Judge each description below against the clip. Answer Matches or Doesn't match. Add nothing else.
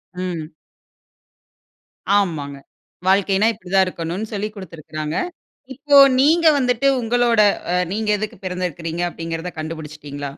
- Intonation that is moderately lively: Matches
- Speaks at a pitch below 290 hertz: Matches